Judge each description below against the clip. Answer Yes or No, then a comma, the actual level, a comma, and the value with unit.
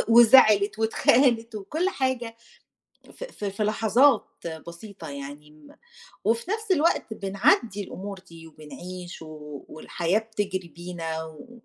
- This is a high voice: Yes, high, 200 Hz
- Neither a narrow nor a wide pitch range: No, wide, 6.0 semitones